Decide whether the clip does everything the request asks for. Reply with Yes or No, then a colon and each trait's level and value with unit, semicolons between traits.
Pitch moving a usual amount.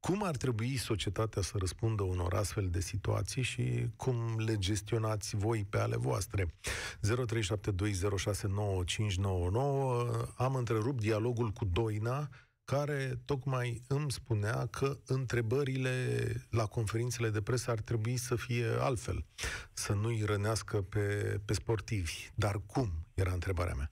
Yes: average, 3.2 semitones